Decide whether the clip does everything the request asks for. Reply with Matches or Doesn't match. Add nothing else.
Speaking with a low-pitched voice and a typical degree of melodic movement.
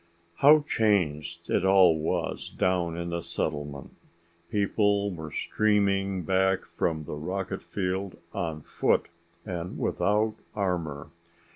Matches